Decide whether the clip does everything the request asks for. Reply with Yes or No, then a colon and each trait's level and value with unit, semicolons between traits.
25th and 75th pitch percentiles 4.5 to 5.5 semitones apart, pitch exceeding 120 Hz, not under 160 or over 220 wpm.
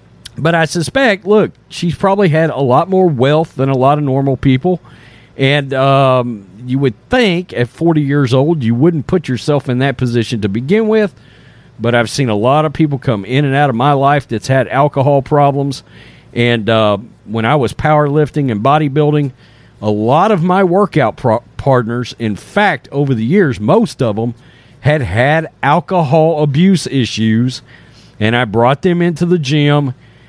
Yes: average, 4.9 semitones; medium, 140 Hz; average, 175 wpm